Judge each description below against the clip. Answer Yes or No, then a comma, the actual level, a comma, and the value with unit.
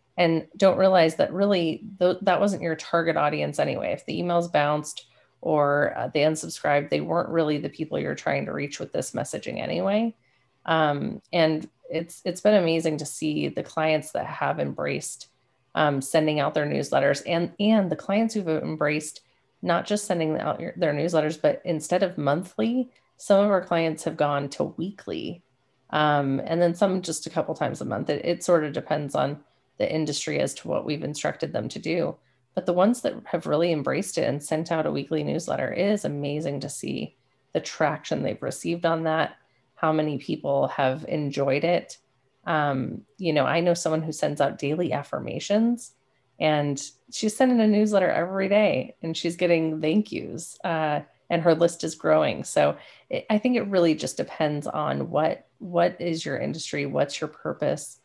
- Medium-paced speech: Yes, average, 185 wpm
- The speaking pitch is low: No, medium, 160 Hz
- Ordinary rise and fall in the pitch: Yes, average, 3.6 semitones